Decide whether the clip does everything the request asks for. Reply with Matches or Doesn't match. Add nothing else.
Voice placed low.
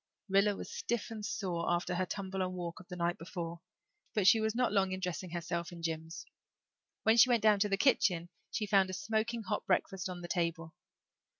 Doesn't match